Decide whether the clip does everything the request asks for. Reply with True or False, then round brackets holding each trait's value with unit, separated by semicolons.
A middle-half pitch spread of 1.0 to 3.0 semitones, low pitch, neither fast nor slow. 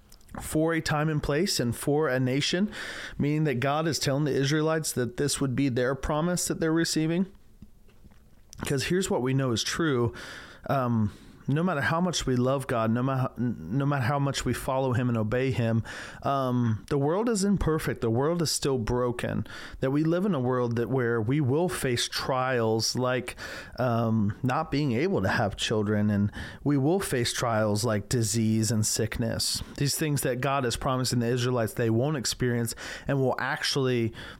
False (4.0 semitones; 130 Hz; 185 wpm)